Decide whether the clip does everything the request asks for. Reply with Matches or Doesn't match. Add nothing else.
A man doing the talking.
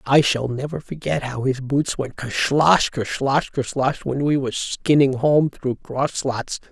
Matches